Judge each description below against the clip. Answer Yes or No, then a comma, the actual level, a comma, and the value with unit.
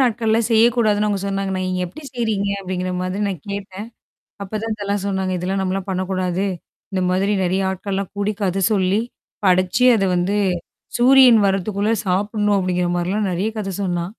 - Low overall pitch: No, high, 195 Hz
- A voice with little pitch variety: Yes, narrow, 2.2 semitones